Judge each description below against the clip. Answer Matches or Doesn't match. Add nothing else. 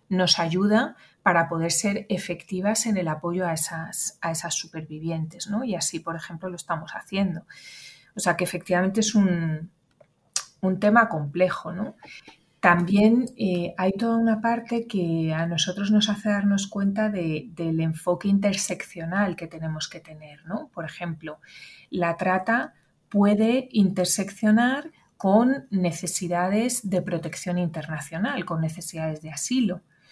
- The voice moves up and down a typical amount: Matches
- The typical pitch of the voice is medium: Matches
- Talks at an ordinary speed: Matches